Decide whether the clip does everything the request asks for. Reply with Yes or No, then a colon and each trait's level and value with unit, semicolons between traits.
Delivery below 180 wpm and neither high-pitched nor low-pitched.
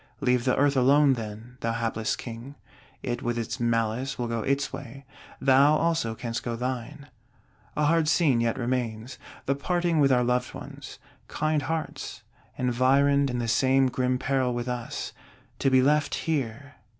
No: average, 160 wpm; low, 130 Hz